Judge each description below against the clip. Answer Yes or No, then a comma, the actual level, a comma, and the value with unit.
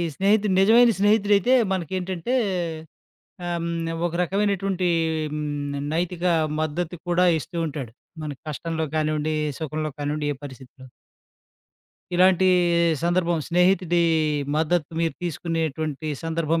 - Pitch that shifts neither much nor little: Yes, average, 3.2 semitones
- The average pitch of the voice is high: No, medium, 170 Hz